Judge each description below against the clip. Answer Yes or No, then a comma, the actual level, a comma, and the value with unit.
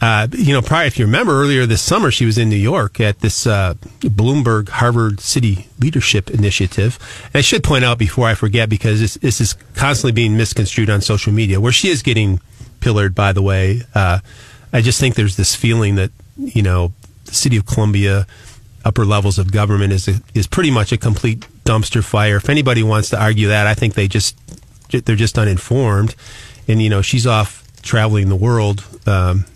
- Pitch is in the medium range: No, low, 110 Hz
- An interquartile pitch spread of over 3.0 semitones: No, narrow, 2.6 semitones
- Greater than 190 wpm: Yes, average, 200 wpm